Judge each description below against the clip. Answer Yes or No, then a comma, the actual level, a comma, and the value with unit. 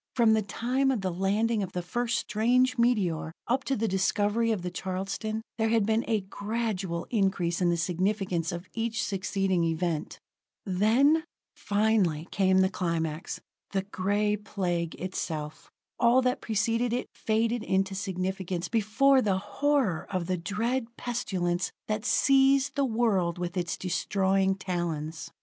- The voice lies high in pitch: Yes, high, 200 Hz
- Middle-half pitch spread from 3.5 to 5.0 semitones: Yes, average, 4.1 semitones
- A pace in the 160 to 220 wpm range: No, average, 145 wpm